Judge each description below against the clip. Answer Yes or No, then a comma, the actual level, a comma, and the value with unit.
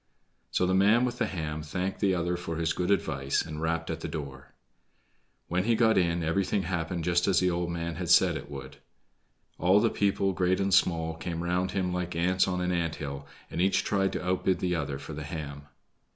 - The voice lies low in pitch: Yes, very low, 90 Hz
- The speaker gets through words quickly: Yes, fast, 215 wpm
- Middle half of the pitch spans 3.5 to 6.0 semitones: No, narrow, 2.4 semitones